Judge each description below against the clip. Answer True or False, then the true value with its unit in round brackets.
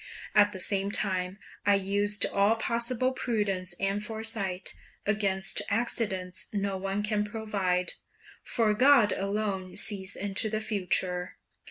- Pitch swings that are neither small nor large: False (2.1 semitones)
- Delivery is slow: True (125 wpm)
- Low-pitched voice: False (205 Hz)